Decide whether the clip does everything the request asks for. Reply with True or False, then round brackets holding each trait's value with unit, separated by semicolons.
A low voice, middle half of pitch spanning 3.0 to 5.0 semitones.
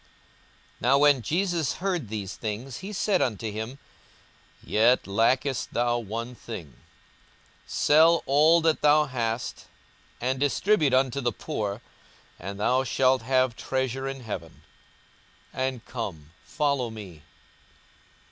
True (130 Hz; 4.0 semitones)